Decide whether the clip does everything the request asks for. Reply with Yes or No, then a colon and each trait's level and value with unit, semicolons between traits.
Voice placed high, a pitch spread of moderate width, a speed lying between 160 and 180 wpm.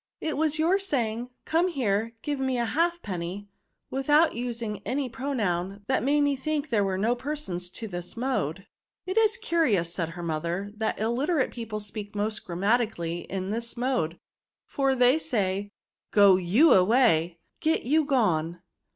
No: high, 230 Hz; wide, 6.6 semitones; average, 170 wpm